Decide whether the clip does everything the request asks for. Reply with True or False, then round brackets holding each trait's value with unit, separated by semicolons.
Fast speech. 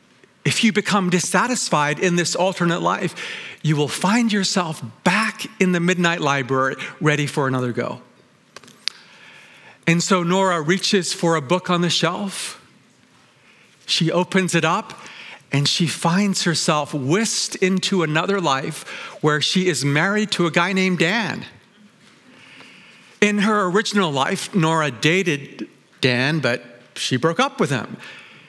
False (135 wpm)